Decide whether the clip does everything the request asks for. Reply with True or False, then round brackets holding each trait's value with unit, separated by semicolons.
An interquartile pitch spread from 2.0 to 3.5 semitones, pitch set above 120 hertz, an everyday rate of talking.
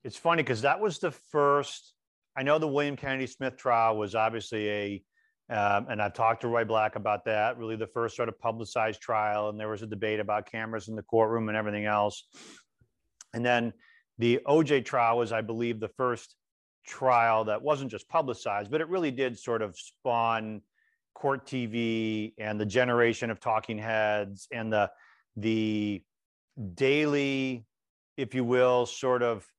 False (3.2 semitones; 115 Hz; 170 wpm)